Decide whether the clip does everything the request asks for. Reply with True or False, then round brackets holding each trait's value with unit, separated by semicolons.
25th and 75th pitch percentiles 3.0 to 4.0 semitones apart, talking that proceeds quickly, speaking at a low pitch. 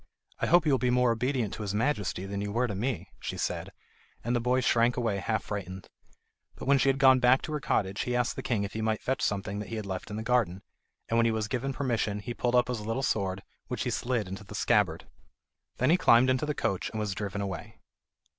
True (3.7 semitones; 250 wpm; 115 Hz)